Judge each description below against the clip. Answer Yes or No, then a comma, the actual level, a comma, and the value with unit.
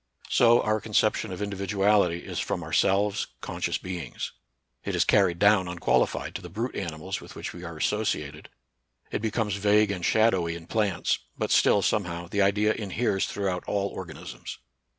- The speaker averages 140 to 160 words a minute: No, average, 170 wpm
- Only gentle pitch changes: No, average, 3.1 semitones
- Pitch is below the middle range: Yes, low, 100 Hz